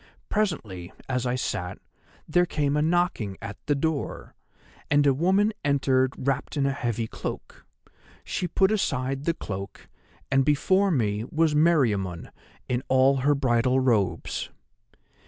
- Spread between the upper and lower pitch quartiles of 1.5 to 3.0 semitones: No, average, 4.7 semitones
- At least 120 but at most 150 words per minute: Yes, slow, 135 wpm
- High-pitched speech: No, low, 135 Hz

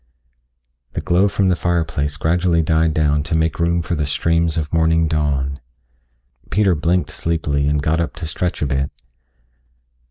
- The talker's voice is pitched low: Yes, very low, 80 Hz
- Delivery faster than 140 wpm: Yes, average, 160 wpm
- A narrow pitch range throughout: Yes, narrow, 2.3 semitones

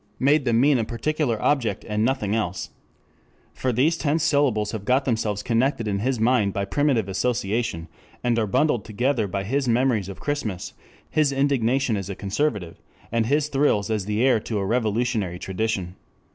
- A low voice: Yes, low, 115 Hz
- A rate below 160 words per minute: No, average, 175 wpm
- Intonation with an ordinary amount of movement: Yes, average, 4.6 semitones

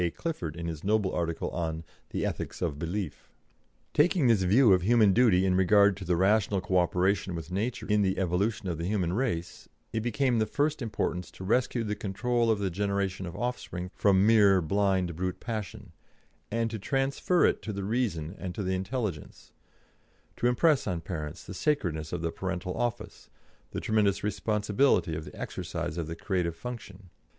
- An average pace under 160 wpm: No, average, 180 wpm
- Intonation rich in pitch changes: No, average, 4.0 semitones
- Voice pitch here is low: Yes, low, 100 Hz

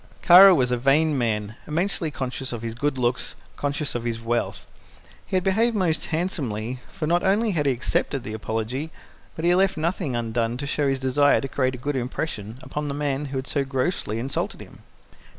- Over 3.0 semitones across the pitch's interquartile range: Yes, average, 4.8 semitones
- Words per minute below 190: No, average, 200 wpm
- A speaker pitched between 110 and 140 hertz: Yes, low, 135 Hz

